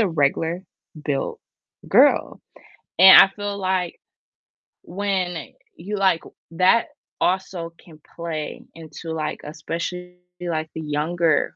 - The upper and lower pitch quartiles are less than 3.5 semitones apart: Yes, average, 2.7 semitones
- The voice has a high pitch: No, medium, 170 Hz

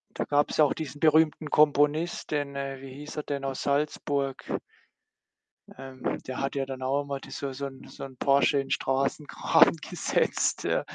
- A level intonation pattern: Yes, narrow, 1.5 semitones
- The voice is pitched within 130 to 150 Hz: Yes, medium, 140 Hz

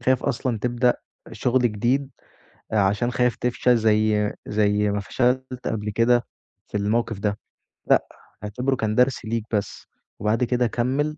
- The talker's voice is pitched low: Yes, low, 115 Hz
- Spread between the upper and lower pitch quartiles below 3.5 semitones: Yes, average, 2.8 semitones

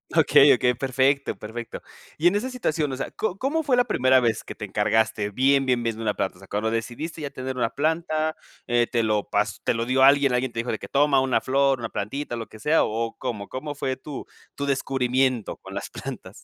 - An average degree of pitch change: Yes, average, 3.6 semitones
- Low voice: Yes, low, 130 Hz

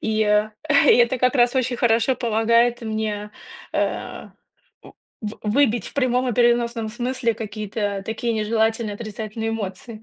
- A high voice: Yes, high, 225 Hz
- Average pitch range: No, narrow, 2.0 semitones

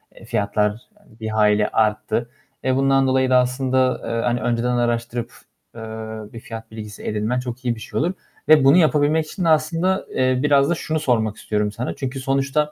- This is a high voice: No, low, 125 Hz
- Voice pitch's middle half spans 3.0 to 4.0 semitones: Yes, average, 3.5 semitones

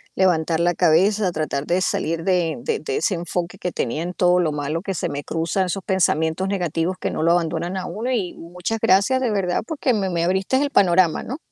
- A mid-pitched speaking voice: Yes, medium, 180 Hz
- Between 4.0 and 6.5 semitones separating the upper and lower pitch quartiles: No, average, 2.9 semitones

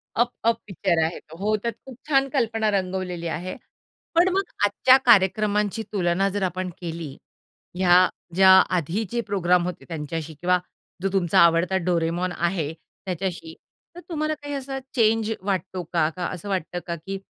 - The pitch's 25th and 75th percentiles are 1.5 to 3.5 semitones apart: No, average, 3.9 semitones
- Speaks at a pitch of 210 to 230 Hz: No, medium, 185 Hz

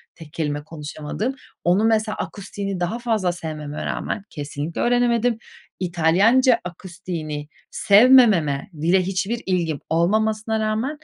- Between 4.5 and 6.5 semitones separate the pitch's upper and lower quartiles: Yes, average, 5.3 semitones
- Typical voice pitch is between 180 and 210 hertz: Yes, high, 190 Hz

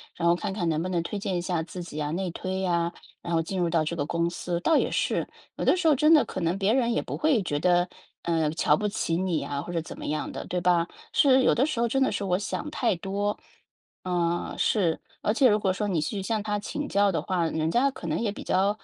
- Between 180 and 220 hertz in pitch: Yes, medium, 185 Hz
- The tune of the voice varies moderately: Yes, average, 3.9 semitones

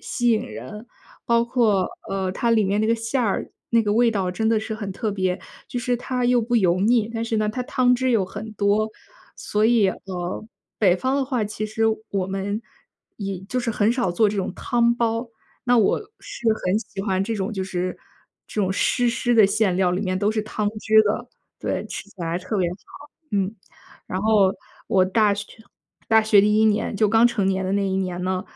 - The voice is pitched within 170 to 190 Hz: No, high, 215 Hz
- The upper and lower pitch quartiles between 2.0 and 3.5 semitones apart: Yes, average, 3.1 semitones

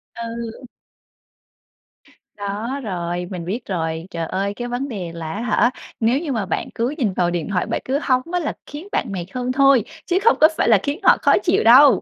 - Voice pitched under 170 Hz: No, high, 230 Hz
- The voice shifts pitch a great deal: Yes, wide, 6.1 semitones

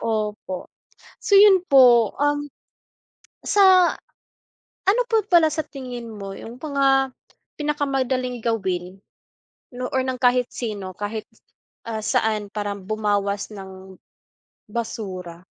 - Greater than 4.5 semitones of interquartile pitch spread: Yes, average, 5.2 semitones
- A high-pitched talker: Yes, high, 235 Hz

